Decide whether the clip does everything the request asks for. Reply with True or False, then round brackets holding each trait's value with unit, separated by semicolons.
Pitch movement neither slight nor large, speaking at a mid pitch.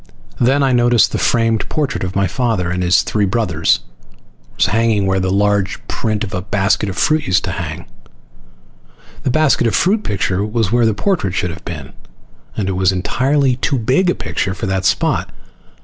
False (4.5 semitones; 105 Hz)